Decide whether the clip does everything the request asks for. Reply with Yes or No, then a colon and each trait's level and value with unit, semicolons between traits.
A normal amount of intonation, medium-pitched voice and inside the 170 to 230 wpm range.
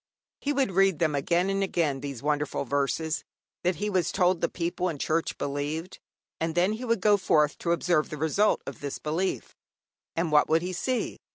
Yes: average, 3.8 semitones; medium, 170 Hz; average, 195 wpm